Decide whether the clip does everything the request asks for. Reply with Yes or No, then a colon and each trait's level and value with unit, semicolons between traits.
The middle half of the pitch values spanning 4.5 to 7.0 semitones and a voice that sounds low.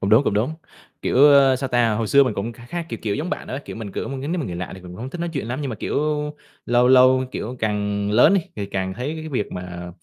Yes: average, 5.0 semitones; low, 120 Hz